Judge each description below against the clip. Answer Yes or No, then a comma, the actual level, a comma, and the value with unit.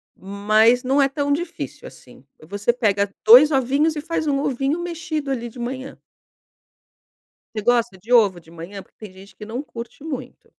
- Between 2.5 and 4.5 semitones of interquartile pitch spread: No, average, 5.1 semitones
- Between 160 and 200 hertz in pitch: No, high, 245 Hz